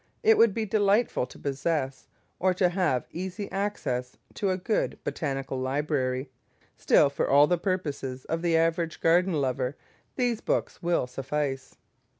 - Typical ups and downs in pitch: No, wide, 5.7 semitones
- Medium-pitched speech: Yes, medium, 165 Hz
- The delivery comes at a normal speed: Yes, average, 150 wpm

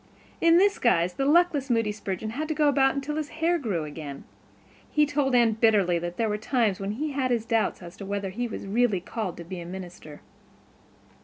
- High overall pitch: Yes, high, 225 Hz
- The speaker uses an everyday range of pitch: No, wide, 6.8 semitones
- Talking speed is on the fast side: Yes, fast, 215 wpm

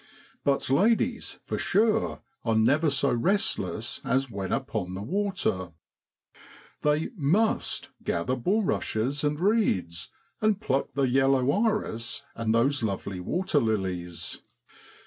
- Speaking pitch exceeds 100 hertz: Yes, low, 135 Hz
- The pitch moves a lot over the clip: Yes, wide, 8.8 semitones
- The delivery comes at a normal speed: No, slow, 110 wpm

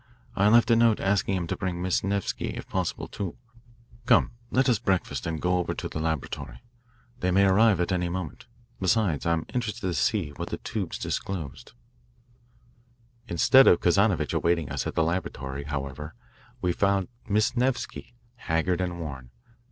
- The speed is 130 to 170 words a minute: Yes, average, 165 wpm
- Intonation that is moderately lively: Yes, average, 3.8 semitones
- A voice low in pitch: Yes, very low, 90 Hz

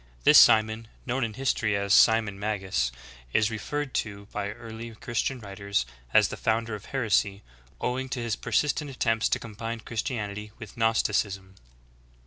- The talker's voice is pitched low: Yes, low, 110 Hz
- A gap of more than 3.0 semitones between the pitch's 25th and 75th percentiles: No, narrow, 2.5 semitones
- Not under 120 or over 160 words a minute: Yes, average, 150 wpm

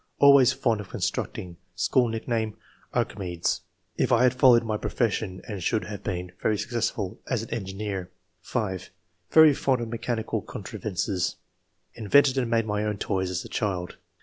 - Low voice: Yes, low, 110 Hz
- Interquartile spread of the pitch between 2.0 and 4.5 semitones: Yes, average, 3.8 semitones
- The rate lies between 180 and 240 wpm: No, average, 160 wpm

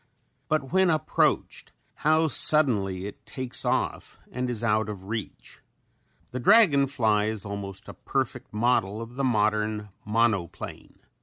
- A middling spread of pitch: Yes, average, 4.5 semitones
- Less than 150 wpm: Yes, slow, 135 wpm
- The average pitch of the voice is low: Yes, low, 115 Hz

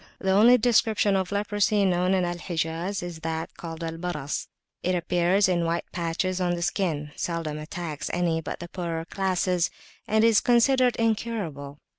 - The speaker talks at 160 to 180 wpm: Yes, average, 165 wpm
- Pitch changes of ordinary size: Yes, average, 3.5 semitones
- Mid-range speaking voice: Yes, medium, 180 Hz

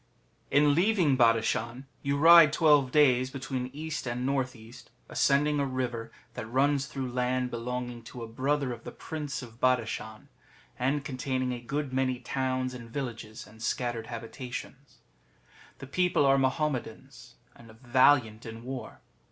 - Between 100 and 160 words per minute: Yes, average, 150 wpm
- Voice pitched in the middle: No, low, 130 Hz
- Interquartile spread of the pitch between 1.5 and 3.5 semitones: Yes, average, 2.7 semitones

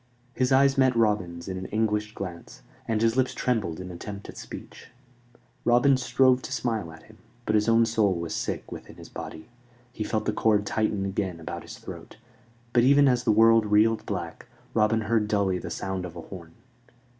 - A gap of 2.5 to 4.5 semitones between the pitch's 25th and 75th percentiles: Yes, average, 3.5 semitones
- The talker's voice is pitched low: Yes, low, 105 Hz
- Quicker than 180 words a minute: Yes, average, 190 wpm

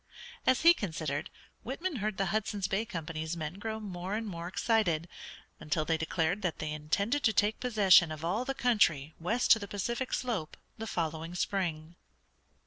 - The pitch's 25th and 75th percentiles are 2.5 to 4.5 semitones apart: No, wide, 5.5 semitones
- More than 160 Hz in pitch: Yes, high, 190 Hz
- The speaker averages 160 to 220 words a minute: Yes, average, 170 wpm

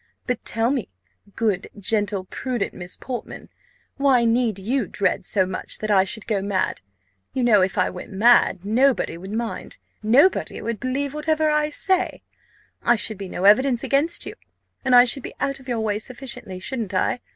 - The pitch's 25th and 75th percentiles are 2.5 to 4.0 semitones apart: No, average, 4.6 semitones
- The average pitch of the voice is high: Yes, high, 230 Hz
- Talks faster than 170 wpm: Yes, average, 180 wpm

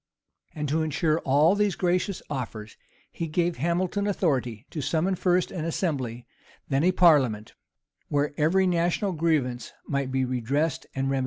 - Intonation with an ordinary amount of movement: Yes, average, 4.7 semitones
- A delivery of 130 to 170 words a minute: Yes, average, 155 wpm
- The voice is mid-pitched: Yes, medium, 155 Hz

